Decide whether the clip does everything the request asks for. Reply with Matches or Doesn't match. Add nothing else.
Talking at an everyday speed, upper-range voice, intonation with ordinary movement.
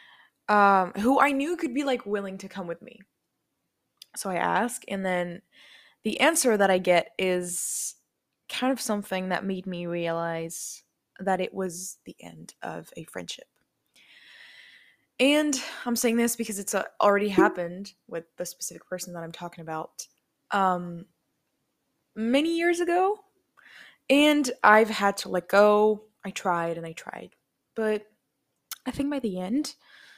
Doesn't match